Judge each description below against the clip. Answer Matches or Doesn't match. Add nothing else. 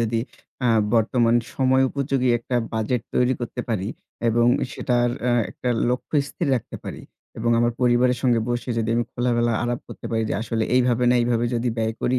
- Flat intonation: Matches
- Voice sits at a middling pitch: Doesn't match